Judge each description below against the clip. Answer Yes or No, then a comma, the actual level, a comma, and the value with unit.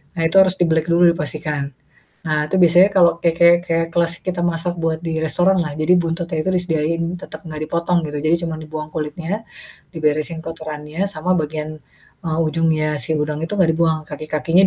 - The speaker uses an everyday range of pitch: No, narrow, 1.8 semitones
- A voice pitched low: No, medium, 165 Hz